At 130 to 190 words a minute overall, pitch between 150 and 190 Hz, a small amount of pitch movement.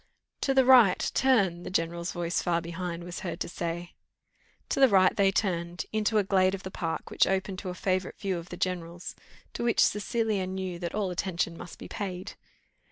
No: fast, 205 wpm; medium, 185 Hz; narrow, 2.3 semitones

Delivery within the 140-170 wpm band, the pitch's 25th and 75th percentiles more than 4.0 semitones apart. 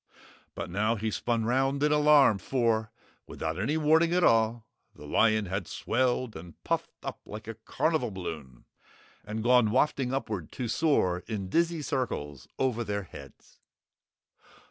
Yes: average, 145 wpm; average, 5.1 semitones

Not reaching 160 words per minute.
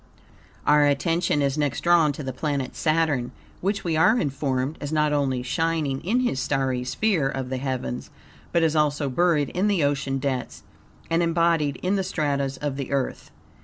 No: average, 175 wpm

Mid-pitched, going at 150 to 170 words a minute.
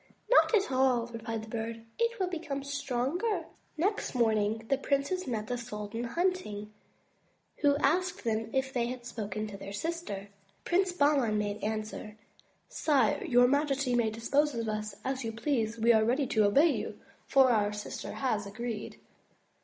No: high, 240 Hz; average, 160 wpm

